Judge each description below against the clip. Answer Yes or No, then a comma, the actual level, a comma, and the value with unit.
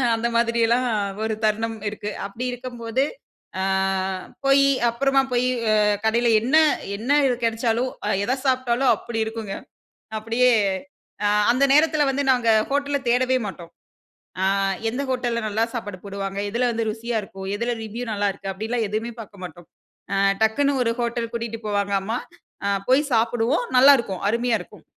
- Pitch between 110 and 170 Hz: No, high, 235 Hz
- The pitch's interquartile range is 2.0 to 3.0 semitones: Yes, narrow, 2.5 semitones